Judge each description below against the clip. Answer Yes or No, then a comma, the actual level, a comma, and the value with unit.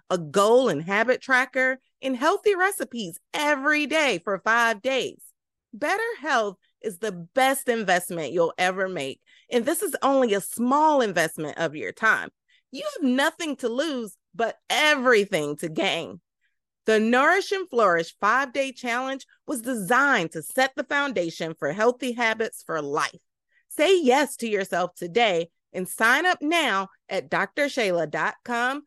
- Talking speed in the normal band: Yes, average, 145 wpm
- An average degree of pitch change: No, wide, 7.0 semitones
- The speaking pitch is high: Yes, high, 245 Hz